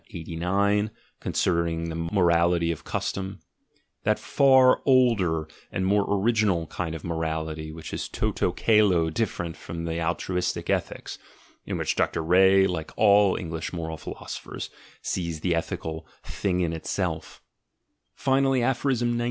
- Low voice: Yes, very low, 90 Hz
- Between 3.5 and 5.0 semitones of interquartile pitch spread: Yes, average, 3.9 semitones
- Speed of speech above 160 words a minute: No, slow, 135 wpm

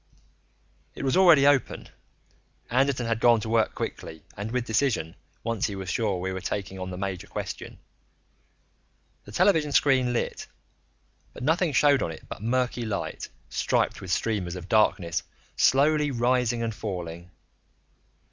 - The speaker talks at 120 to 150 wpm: Yes, average, 145 wpm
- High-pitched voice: No, low, 115 Hz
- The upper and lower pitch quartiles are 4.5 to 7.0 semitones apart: Yes, wide, 5.5 semitones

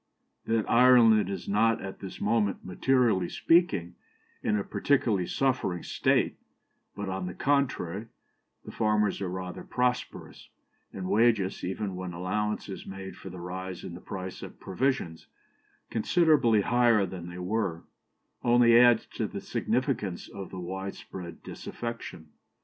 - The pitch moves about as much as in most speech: Yes, average, 4.2 semitones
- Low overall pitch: Yes, low, 100 Hz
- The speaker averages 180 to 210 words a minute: No, average, 140 wpm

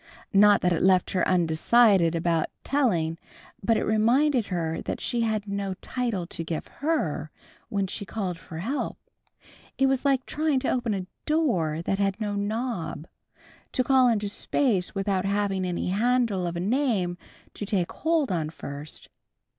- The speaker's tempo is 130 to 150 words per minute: No, average, 160 wpm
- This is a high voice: Yes, high, 200 Hz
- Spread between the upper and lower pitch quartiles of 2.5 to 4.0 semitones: No, wide, 5.5 semitones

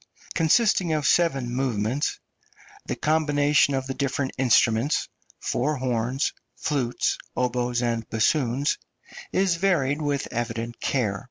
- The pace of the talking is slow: Yes, slow, 110 wpm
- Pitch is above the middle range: No, low, 135 Hz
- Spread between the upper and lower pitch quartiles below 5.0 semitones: Yes, average, 3.8 semitones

